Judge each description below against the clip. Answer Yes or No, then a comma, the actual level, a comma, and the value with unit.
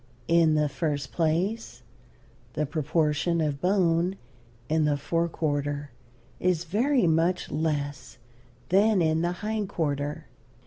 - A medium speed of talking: No, slow, 120 wpm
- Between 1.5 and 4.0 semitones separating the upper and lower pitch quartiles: Yes, average, 3.3 semitones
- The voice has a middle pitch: Yes, medium, 160 Hz